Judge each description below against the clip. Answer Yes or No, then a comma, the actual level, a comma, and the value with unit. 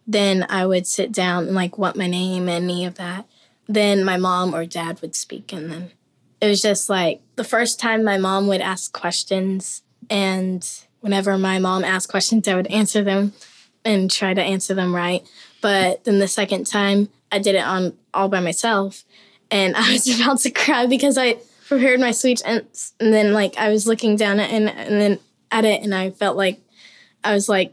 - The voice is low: No, high, 195 Hz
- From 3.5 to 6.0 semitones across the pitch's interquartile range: No, narrow, 2.5 semitones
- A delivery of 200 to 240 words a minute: Yes, fast, 205 wpm